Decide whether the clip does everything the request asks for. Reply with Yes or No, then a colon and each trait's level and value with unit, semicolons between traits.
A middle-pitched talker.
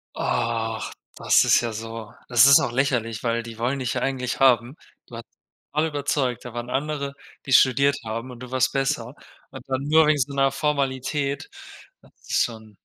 No: low, 130 Hz